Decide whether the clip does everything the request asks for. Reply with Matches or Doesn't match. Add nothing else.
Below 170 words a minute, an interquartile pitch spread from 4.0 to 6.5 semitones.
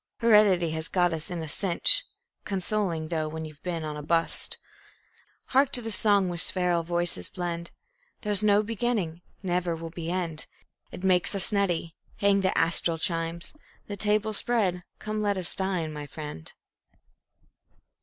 Doesn't match